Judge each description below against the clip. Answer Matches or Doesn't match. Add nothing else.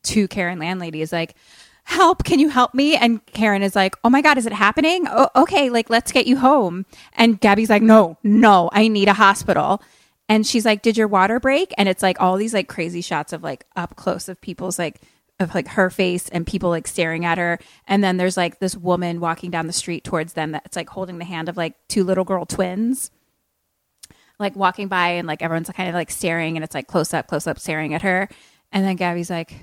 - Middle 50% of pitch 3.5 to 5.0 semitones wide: Matches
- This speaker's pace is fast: Matches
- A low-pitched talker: Doesn't match